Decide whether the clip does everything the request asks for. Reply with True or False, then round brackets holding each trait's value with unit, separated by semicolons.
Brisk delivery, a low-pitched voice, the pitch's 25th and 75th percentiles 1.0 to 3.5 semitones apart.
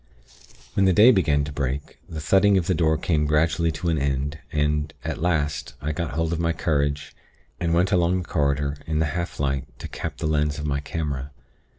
True (210 wpm; 75 Hz; 2.7 semitones)